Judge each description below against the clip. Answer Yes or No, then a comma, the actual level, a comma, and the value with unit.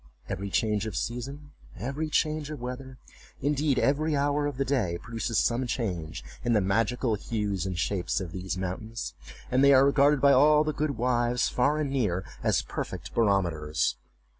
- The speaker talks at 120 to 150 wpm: No, average, 170 wpm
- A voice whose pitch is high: No, low, 125 Hz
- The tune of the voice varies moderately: No, wide, 5.9 semitones